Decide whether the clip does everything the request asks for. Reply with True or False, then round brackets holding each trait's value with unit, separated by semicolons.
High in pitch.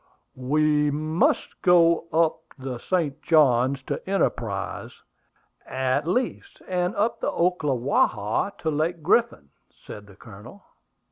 False (150 Hz)